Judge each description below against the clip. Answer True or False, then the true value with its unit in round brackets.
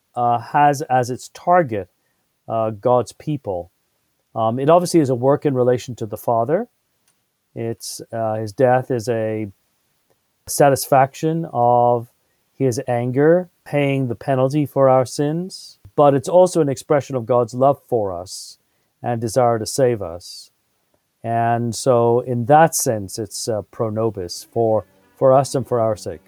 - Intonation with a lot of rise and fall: False (3.8 semitones)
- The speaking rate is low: False (150 wpm)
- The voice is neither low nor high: False (125 Hz)